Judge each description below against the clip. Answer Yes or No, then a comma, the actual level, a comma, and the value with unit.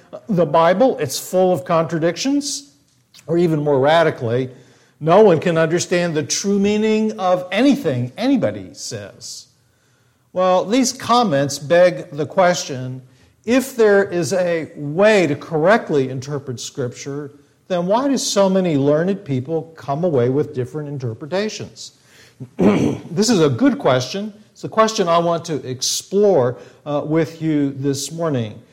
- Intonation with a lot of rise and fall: Yes, wide, 5.9 semitones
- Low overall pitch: No, medium, 160 Hz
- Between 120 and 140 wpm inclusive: Yes, slow, 135 wpm